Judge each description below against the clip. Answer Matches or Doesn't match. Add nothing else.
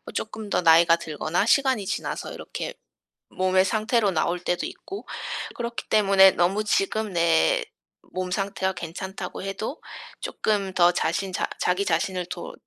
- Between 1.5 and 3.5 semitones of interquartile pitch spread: Matches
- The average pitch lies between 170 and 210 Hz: Matches